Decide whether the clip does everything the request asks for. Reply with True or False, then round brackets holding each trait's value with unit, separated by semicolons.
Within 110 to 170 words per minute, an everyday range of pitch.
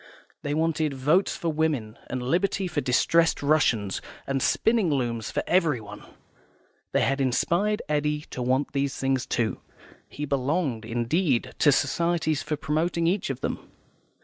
True (145 wpm; 4.4 semitones)